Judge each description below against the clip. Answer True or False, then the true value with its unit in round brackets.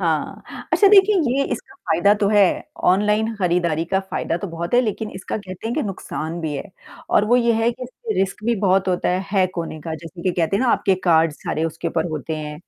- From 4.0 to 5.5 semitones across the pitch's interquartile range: True (4.9 semitones)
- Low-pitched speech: False (190 Hz)